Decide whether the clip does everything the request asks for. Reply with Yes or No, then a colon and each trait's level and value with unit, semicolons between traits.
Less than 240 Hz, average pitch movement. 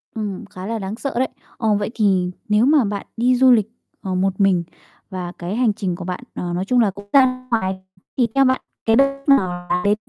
Yes: high, 210 Hz; average, 4.7 semitones